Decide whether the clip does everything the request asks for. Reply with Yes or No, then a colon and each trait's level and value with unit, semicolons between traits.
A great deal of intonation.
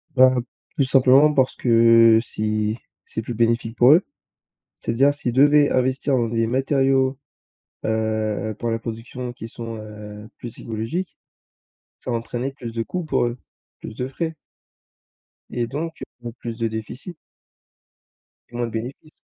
No: average, 2.8 semitones